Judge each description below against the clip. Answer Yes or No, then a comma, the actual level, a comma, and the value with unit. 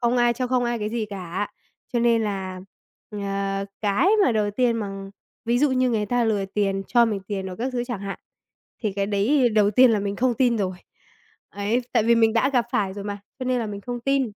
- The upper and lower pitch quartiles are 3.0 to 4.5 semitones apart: Yes, average, 3.3 semitones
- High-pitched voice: Yes, high, 220 Hz